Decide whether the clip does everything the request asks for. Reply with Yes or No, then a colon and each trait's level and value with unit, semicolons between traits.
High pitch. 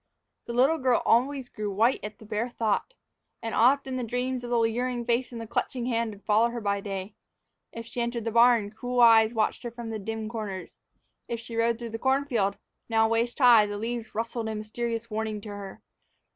Yes: high, 230 Hz